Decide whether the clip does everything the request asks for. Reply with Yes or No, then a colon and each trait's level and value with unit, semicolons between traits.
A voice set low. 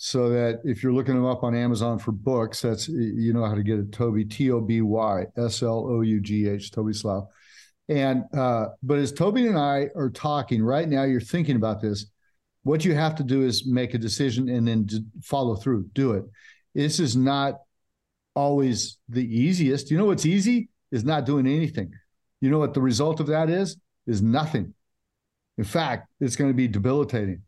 Yes: low, 125 Hz